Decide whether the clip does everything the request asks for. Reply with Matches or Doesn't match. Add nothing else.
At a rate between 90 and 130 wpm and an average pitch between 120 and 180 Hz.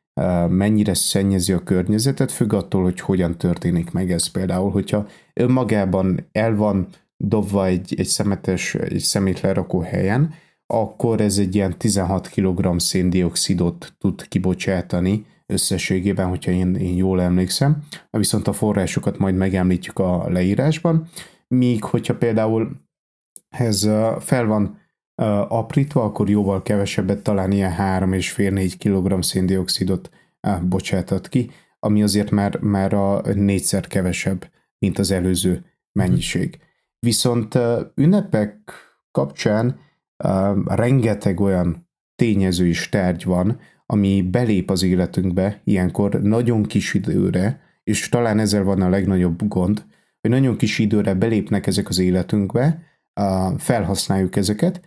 Doesn't match